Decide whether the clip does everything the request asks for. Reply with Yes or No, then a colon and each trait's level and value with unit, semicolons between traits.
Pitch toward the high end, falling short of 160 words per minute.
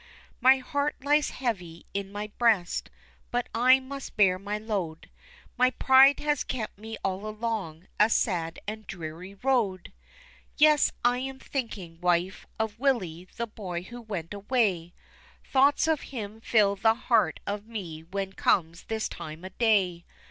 Yes: high, 210 Hz; average, 150 wpm